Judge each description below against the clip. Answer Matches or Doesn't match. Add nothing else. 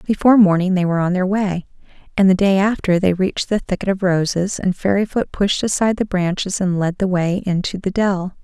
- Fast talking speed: Matches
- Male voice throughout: Doesn't match